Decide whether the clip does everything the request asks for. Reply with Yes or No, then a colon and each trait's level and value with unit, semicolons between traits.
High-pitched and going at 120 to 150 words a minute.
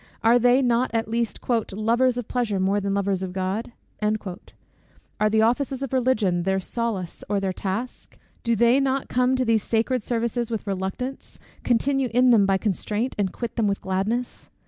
No: high, 225 Hz; average, 175 wpm